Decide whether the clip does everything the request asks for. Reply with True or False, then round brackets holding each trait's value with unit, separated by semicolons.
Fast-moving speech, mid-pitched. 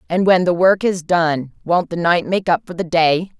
True (230 wpm; 175 Hz)